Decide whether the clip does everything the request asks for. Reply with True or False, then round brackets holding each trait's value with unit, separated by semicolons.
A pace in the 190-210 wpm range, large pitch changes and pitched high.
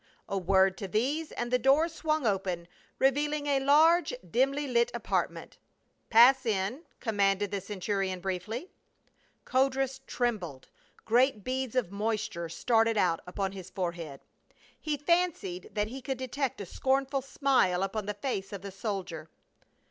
False (145 wpm; 5.8 semitones; 225 Hz)